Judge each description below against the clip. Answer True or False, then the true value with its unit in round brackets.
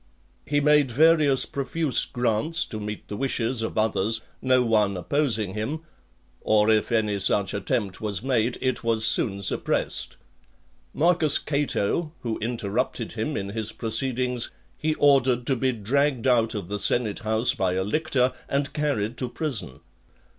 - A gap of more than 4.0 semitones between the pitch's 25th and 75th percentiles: True (4.5 semitones)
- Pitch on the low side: True (120 Hz)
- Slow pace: False (150 wpm)